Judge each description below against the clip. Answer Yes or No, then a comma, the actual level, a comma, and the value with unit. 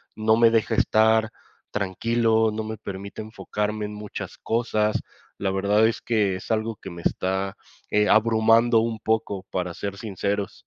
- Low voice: Yes, low, 110 Hz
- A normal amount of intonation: No, narrow, 2.0 semitones